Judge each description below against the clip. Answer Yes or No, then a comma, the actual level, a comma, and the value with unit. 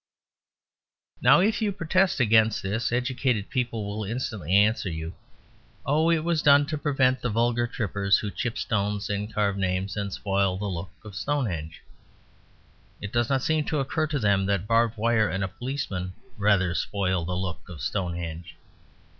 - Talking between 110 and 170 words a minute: Yes, average, 165 wpm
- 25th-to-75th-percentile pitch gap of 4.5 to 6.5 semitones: Yes, average, 4.9 semitones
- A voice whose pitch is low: Yes, low, 105 Hz